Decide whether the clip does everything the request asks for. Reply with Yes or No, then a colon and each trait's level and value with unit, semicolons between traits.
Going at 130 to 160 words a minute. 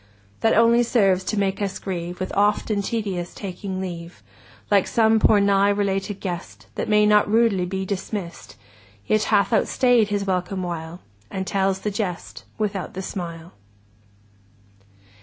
Yes: average, 155 wpm